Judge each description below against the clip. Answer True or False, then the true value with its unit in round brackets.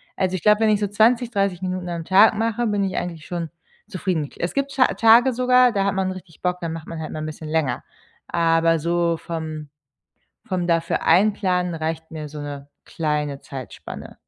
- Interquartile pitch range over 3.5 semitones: True (4.2 semitones)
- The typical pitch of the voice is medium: True (175 Hz)